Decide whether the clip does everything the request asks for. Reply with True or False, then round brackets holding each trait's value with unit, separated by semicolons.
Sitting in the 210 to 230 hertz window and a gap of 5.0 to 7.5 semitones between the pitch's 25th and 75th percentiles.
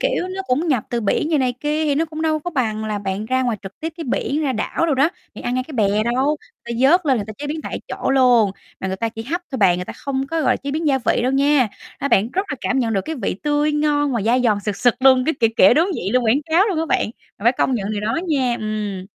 False (255 Hz; 5.3 semitones)